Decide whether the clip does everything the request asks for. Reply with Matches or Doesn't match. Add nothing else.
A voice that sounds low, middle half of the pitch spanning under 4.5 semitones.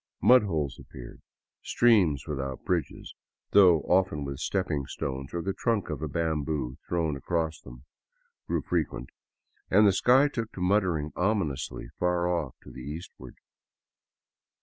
Doesn't match